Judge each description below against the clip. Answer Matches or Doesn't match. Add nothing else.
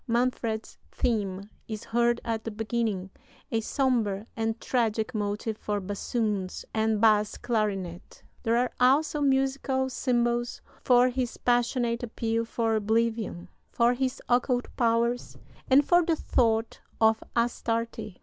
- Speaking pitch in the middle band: Doesn't match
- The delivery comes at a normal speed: Doesn't match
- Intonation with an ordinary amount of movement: Doesn't match